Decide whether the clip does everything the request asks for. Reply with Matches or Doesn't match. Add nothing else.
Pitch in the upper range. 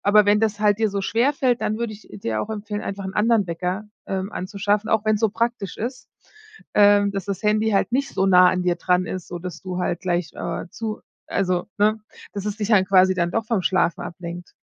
Matches